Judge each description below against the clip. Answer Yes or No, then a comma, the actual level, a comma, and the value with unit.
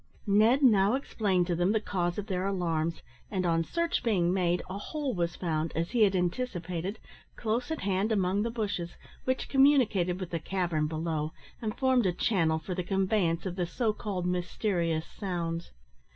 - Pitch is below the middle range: No, medium, 185 Hz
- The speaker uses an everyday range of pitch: Yes, average, 3.9 semitones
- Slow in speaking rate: No, average, 180 wpm